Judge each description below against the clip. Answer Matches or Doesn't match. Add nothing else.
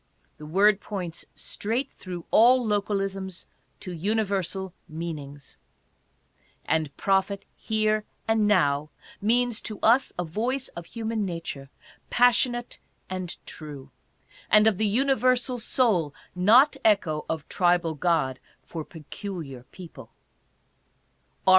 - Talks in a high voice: Matches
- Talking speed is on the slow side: Matches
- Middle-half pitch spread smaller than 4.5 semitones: Doesn't match